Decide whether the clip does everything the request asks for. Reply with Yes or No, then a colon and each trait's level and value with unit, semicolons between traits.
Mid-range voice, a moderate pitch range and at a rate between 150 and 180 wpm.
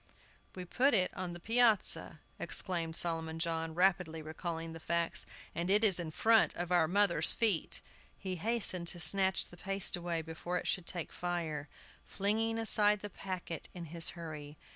Yes: medium, 175 Hz; average, 3.1 semitones; average, 165 wpm